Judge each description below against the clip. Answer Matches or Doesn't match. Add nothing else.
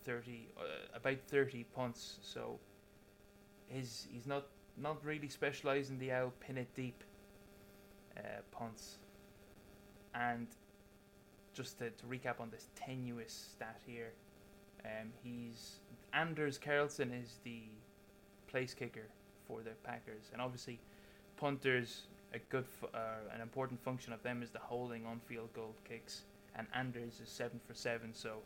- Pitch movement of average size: Doesn't match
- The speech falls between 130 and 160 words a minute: Matches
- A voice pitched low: Matches